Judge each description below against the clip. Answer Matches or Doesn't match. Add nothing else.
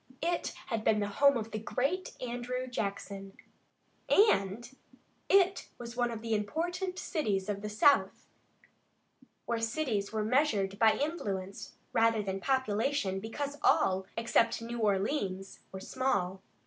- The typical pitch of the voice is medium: Doesn't match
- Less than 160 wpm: Matches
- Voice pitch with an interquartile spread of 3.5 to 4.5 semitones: Doesn't match